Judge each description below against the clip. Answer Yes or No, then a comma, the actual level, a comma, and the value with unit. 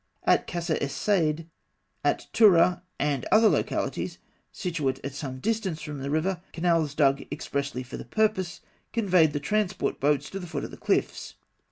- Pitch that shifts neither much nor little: Yes, average, 4.9 semitones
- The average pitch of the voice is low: No, medium, 160 Hz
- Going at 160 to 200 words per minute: Yes, average, 165 wpm